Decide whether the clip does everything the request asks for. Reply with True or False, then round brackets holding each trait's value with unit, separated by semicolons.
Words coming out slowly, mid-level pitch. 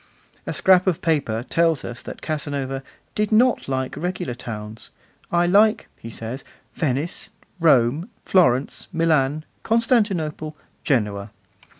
True (115 wpm; 155 Hz)